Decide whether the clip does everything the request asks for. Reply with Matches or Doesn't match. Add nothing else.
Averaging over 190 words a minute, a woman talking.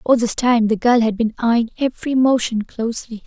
Matches